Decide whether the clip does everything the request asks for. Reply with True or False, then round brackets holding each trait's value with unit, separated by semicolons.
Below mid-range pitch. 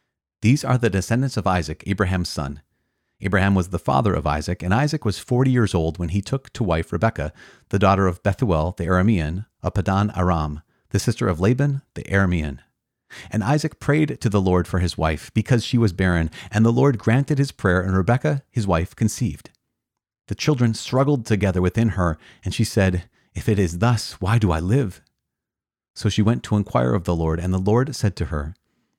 True (100 Hz)